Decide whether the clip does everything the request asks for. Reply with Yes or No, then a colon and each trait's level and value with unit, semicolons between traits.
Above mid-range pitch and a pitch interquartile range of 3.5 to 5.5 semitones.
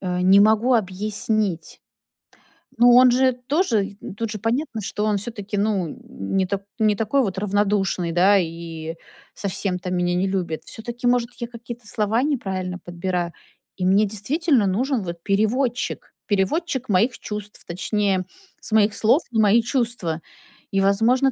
Yes: high, 210 Hz; average, 4.0 semitones